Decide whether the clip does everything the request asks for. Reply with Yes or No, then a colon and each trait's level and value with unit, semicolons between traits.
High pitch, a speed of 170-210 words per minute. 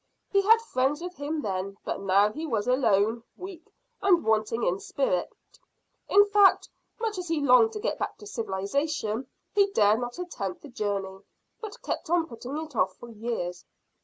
Yes: very high, 255 Hz; average, 175 wpm